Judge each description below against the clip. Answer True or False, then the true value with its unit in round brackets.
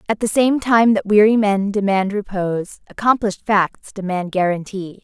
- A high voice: True (205 Hz)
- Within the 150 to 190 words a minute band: True (155 wpm)